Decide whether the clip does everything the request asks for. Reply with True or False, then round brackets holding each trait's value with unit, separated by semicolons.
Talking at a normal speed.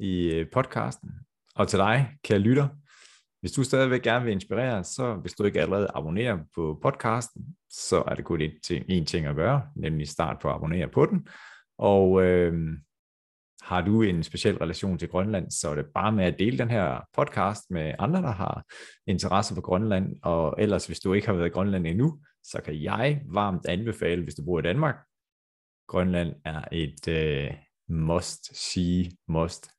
True (175 wpm)